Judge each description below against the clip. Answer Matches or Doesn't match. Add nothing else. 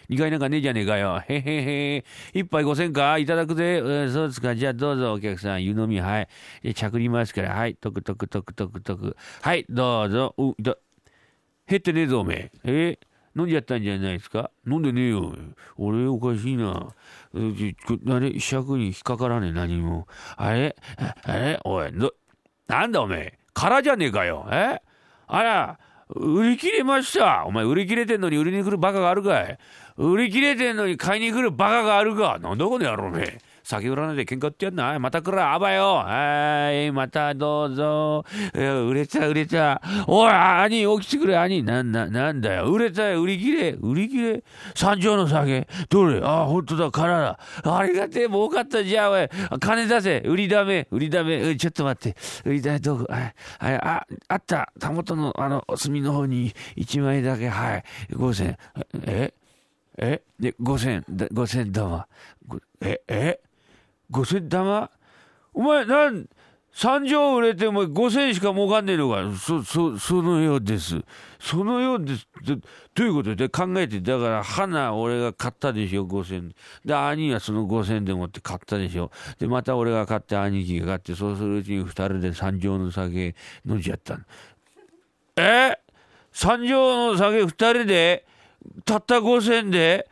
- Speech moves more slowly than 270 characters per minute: Doesn't match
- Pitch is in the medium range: Matches